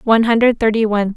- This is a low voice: No, high, 220 Hz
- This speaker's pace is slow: No, fast, 205 wpm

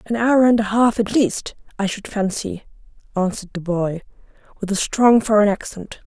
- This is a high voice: Yes, high, 210 Hz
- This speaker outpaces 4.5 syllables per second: Yes, 5.0 syllables/s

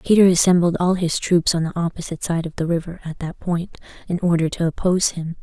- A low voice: No, medium, 170 Hz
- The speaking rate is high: Yes, fast, 220 wpm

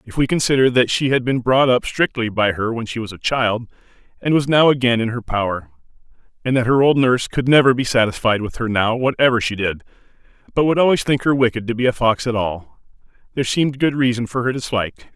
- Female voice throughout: No, male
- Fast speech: Yes, fast, 230 wpm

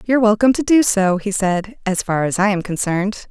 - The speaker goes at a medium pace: No, fast, 235 wpm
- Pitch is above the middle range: Yes, high, 205 Hz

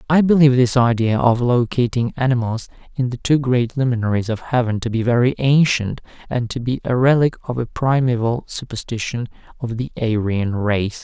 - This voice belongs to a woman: No, male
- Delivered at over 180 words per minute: No, average, 170 wpm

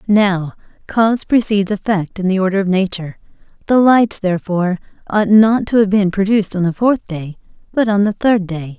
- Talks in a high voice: Yes, high, 200 Hz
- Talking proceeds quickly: No, average, 185 wpm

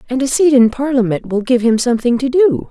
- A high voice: Yes, very high, 250 Hz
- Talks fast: Yes, fast, 245 wpm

